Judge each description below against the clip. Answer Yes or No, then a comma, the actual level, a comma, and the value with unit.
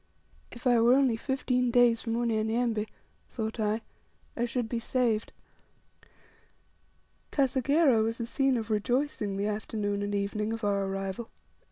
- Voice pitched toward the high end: Yes, high, 230 Hz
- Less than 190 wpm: Yes, average, 140 wpm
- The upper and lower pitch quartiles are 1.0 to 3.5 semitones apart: Yes, average, 2.7 semitones